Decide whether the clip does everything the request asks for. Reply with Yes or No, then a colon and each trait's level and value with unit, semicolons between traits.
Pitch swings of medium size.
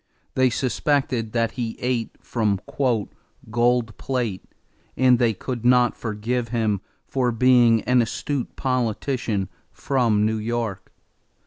No: narrow, 2.2 semitones